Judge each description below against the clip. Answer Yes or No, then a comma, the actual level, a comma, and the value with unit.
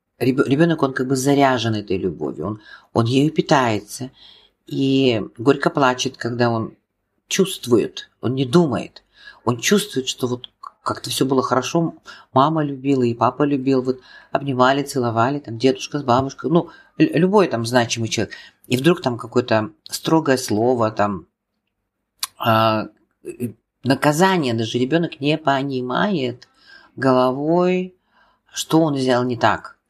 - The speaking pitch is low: Yes, low, 130 Hz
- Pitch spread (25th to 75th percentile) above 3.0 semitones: Yes, average, 3.8 semitones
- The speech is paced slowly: No, average, 130 wpm